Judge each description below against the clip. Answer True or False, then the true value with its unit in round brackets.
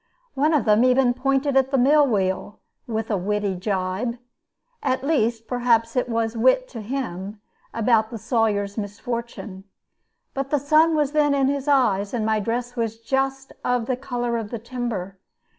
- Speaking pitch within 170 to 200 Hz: False (235 Hz)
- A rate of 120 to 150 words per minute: False (170 wpm)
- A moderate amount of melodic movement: True (3.8 semitones)